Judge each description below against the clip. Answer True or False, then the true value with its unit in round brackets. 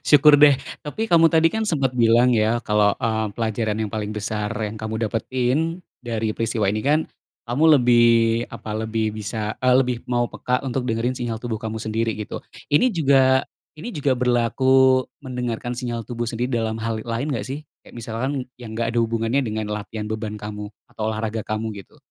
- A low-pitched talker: True (115 Hz)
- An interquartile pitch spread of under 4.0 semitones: True (2.9 semitones)